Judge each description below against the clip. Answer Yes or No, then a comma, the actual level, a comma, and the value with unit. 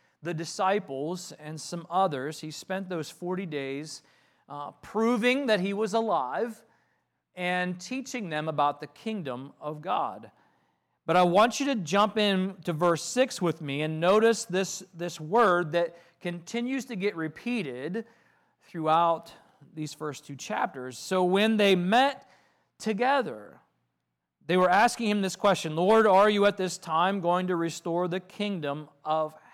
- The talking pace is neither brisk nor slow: Yes, average, 150 wpm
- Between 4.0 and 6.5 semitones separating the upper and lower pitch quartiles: Yes, average, 5.0 semitones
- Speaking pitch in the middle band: Yes, medium, 180 Hz